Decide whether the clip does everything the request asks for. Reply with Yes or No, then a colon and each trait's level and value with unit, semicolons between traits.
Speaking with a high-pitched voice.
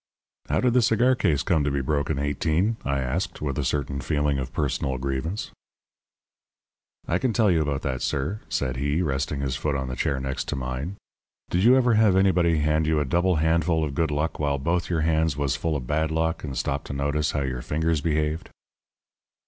No: very low, 75 Hz